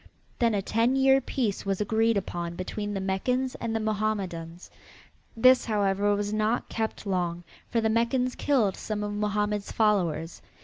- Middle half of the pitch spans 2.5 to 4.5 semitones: Yes, average, 2.8 semitones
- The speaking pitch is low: No, high, 210 Hz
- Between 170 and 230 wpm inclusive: No, average, 160 wpm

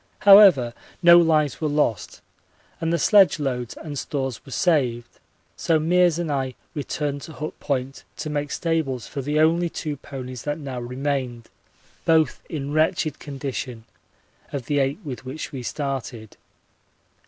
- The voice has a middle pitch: Yes, medium, 145 Hz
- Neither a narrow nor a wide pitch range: Yes, average, 3.3 semitones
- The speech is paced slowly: No, average, 150 wpm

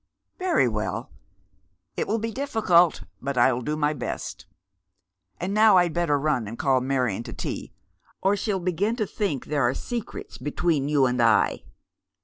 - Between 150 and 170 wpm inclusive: Yes, average, 165 wpm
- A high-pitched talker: No, medium, 150 Hz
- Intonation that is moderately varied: No, wide, 7.7 semitones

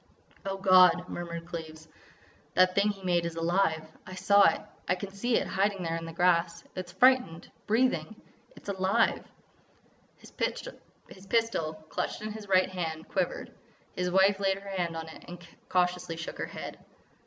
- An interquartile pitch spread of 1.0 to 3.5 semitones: Yes, average, 2.7 semitones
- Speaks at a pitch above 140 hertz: Yes, medium, 185 Hz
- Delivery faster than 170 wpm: No, average, 160 wpm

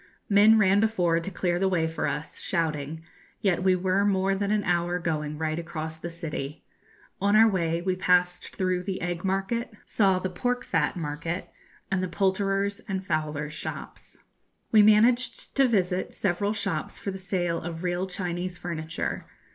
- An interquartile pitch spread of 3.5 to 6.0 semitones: No, average, 2.9 semitones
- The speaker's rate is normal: Yes, average, 170 wpm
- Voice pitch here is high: No, medium, 180 Hz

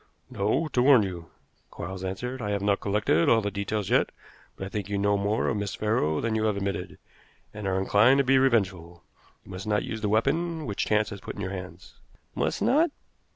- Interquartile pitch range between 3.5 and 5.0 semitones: No, average, 2.8 semitones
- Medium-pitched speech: No, low, 105 Hz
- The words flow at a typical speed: No, fast, 215 wpm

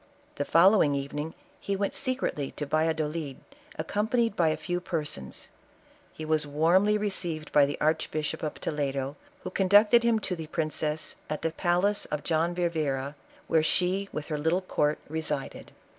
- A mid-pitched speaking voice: Yes, medium, 160 Hz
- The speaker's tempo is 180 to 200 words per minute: No, average, 160 wpm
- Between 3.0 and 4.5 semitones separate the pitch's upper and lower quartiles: Yes, average, 3.6 semitones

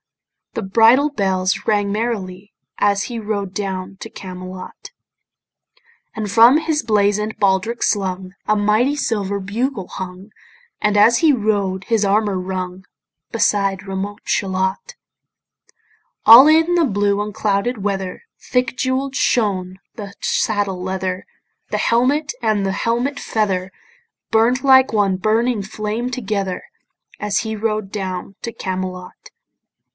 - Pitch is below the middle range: No, high, 205 Hz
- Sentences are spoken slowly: Yes, slow, 125 wpm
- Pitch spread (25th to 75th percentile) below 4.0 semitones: Yes, average, 3.4 semitones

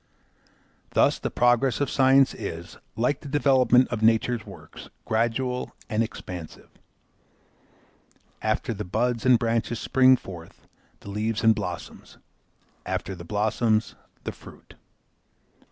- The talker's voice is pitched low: Yes, low, 115 Hz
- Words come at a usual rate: No, slow, 120 wpm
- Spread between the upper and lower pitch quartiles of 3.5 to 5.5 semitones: No, average, 2.8 semitones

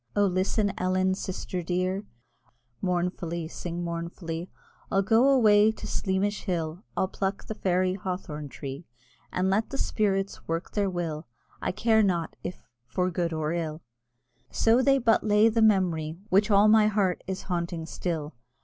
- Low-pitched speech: No, medium, 185 Hz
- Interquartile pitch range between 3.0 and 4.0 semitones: Yes, average, 3.3 semitones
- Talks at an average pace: Yes, average, 155 wpm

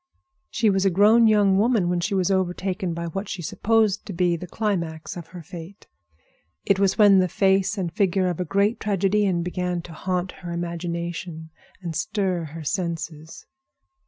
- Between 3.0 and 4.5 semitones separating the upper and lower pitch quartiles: No, narrow, 2.6 semitones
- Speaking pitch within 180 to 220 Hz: Yes, medium, 185 Hz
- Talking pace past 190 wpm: No, average, 175 wpm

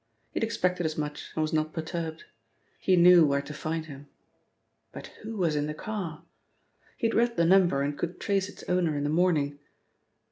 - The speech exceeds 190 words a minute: Yes, average, 200 wpm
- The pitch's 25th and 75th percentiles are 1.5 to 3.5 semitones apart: Yes, average, 3.2 semitones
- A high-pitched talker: No, medium, 165 Hz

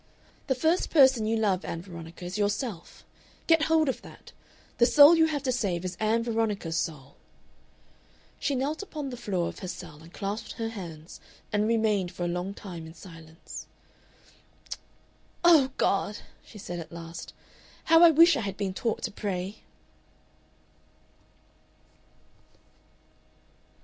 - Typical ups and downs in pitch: No, wide, 6.9 semitones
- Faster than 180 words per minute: No, average, 145 wpm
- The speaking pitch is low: No, high, 210 Hz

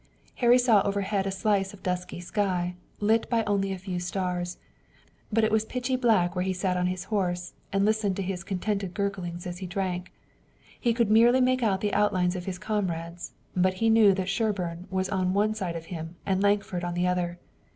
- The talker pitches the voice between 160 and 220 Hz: Yes, high, 190 Hz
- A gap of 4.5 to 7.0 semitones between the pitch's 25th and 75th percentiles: No, average, 2.8 semitones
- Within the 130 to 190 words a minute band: No, fast, 205 wpm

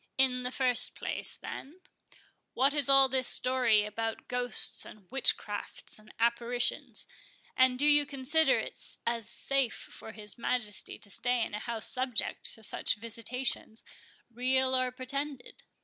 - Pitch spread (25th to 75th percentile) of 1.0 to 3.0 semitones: Yes, narrow, 2.5 semitones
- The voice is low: No, very high, 250 Hz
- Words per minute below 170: Yes, average, 150 wpm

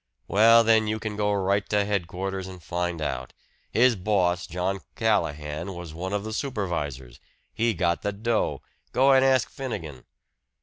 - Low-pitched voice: Yes, low, 100 Hz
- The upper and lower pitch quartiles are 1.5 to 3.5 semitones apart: No, average, 3.9 semitones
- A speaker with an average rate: Yes, average, 160 wpm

